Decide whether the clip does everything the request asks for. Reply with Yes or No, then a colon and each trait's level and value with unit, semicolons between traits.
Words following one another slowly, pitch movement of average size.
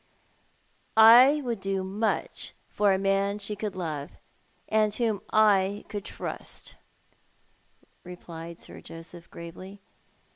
Yes: slow, 120 wpm; average, 3.0 semitones